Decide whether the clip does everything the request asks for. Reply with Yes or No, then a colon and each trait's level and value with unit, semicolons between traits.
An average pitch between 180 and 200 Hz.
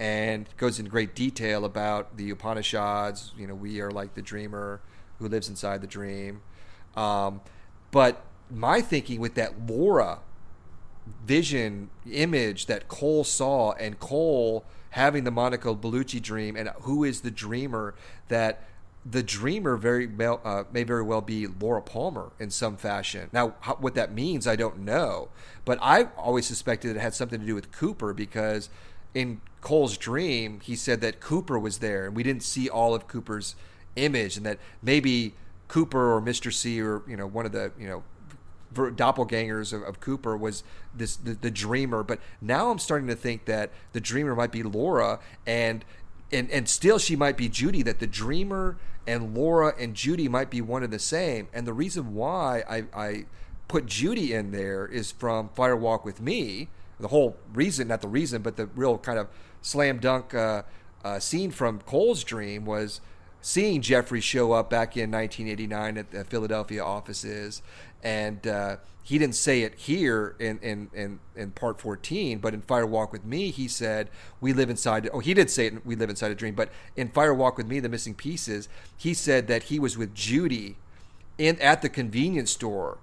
No: low, 110 Hz